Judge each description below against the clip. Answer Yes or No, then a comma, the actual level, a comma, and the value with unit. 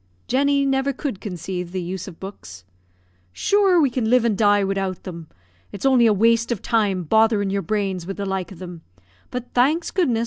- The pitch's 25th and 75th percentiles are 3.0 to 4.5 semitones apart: No, average, 4.9 semitones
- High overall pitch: Yes, high, 205 Hz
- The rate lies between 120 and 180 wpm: No, average, 195 wpm